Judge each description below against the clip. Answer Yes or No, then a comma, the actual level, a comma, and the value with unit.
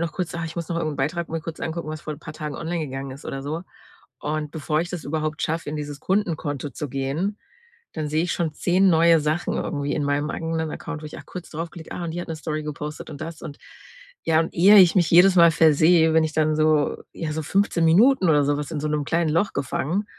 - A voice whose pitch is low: No, medium, 160 Hz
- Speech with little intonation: Yes, narrow, 2.0 semitones